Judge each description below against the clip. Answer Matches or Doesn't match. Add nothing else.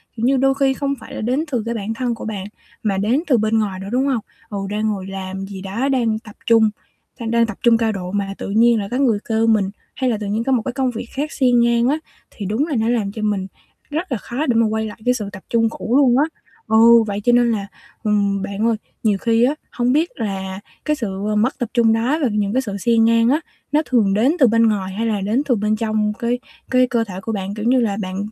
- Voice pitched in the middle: Doesn't match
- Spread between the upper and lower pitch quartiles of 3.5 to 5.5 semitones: Doesn't match